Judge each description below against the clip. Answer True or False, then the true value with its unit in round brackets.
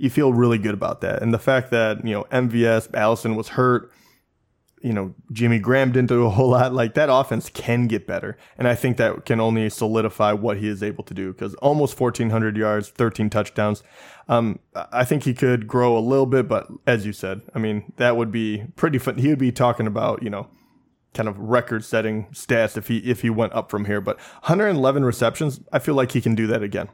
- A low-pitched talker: True (115 Hz)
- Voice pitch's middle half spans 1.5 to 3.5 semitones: True (2.6 semitones)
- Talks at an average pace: False (230 wpm)